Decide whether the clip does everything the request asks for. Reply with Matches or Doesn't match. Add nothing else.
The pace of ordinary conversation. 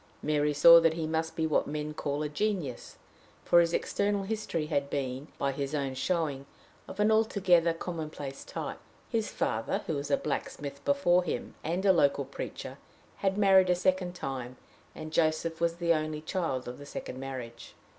Matches